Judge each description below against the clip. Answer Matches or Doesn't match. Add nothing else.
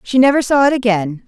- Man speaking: Doesn't match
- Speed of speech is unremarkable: Doesn't match